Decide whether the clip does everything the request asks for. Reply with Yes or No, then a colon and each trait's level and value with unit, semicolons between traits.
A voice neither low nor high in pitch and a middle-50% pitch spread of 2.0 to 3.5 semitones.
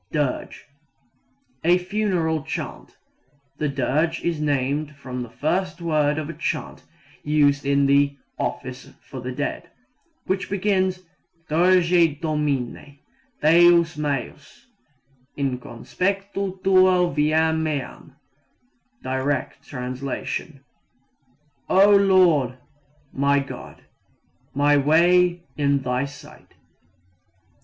No: medium, 150 Hz; average, 4.0 semitones